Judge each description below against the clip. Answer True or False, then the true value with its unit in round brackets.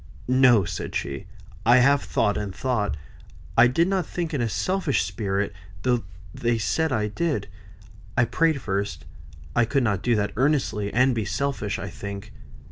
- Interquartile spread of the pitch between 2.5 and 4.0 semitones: False (5.3 semitones)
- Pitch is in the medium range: False (120 Hz)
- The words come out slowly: False (165 wpm)